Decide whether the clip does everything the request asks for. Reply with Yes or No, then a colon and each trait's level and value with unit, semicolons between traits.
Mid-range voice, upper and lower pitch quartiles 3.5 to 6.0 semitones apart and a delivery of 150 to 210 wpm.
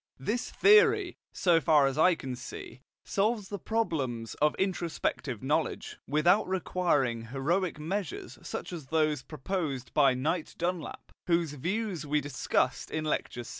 No: medium, 155 Hz; average, 5.3 semitones; average, 140 wpm